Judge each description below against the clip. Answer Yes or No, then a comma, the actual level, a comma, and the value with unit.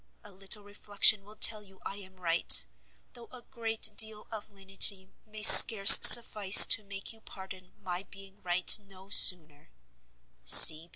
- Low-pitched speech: No, high, 200 Hz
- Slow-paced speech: No, average, 150 wpm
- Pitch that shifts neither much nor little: No, narrow, 2.2 semitones